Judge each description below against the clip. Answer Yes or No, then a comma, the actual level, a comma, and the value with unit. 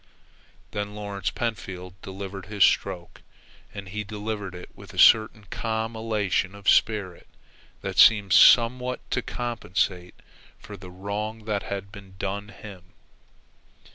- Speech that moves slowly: Yes, slow, 130 wpm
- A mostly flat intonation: Yes, narrow, 2.2 semitones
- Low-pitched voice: Yes, low, 100 Hz